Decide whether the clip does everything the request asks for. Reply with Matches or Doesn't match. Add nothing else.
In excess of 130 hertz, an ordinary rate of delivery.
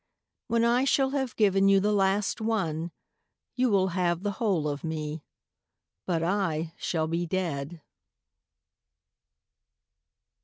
Doesn't match